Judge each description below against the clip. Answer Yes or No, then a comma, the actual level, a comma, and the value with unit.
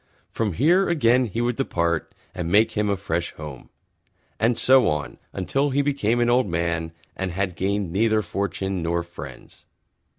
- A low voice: Yes, low, 100 Hz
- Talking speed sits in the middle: Yes, average, 165 wpm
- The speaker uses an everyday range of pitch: No, wide, 5.8 semitones